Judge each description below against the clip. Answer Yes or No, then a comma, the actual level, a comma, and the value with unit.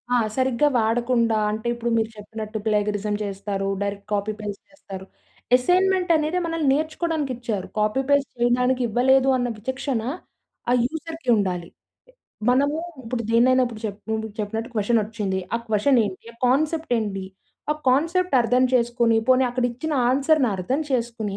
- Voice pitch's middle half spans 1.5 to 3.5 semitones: No, average, 4.2 semitones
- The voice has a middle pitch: No, high, 240 Hz